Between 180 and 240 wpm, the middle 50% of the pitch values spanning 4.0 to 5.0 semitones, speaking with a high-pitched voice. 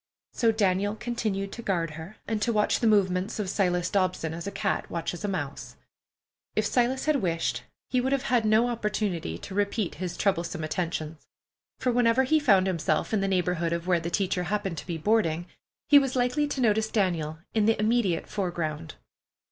Yes: average, 190 wpm; average, 4.7 semitones; high, 195 Hz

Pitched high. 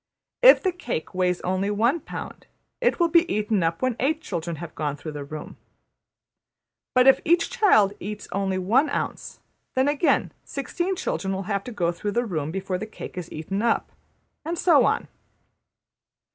Yes: high, 210 Hz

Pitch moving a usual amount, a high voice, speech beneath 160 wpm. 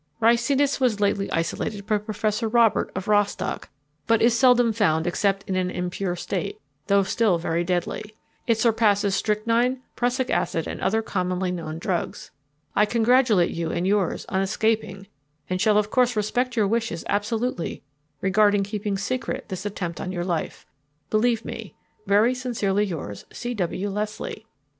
Yes: average, 3.5 semitones; high, 210 Hz; average, 150 wpm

